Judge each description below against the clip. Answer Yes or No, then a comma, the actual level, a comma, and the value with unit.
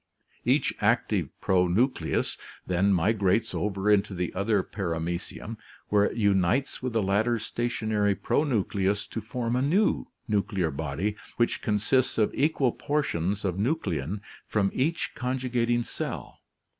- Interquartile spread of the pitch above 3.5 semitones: Yes, average, 4.0 semitones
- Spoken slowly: Yes, slow, 125 wpm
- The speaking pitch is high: No, low, 105 Hz